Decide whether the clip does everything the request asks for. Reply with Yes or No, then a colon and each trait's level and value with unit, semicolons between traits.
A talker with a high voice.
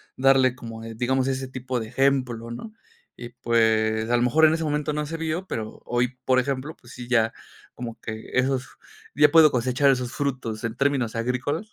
No: low, 130 Hz